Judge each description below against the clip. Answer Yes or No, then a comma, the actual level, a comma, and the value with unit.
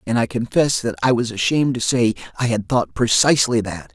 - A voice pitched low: Yes, low, 115 Hz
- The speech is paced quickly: Yes, fast, 215 wpm